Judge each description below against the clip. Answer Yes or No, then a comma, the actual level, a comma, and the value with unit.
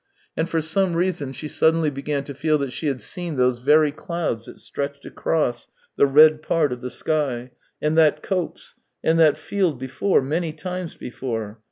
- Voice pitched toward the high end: No, medium, 150 Hz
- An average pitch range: Yes, average, 3.4 semitones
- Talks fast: No, average, 180 wpm